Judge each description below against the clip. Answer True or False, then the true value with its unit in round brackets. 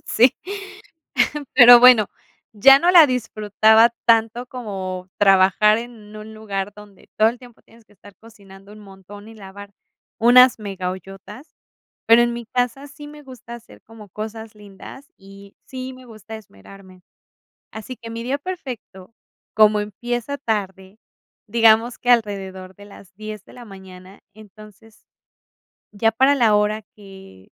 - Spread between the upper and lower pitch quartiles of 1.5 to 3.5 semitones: True (3.2 semitones)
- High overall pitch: True (215 Hz)